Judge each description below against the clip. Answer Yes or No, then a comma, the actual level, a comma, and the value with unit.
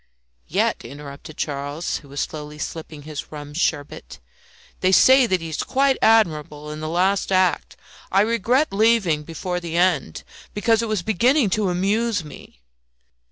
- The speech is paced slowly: No, average, 155 wpm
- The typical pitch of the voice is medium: Yes, medium, 175 Hz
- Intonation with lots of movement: Yes, wide, 6.2 semitones